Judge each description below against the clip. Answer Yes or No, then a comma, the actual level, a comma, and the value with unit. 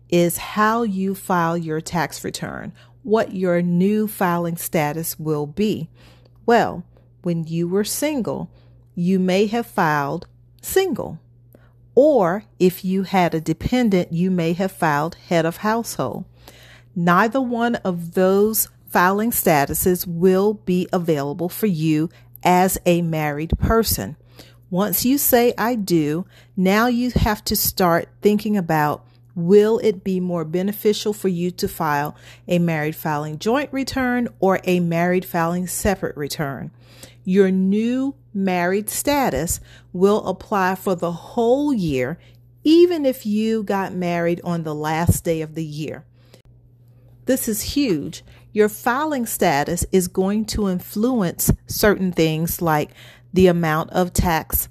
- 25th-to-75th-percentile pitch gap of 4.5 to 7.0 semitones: Yes, average, 5.0 semitones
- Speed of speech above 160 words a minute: No, slow, 135 wpm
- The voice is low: No, medium, 180 Hz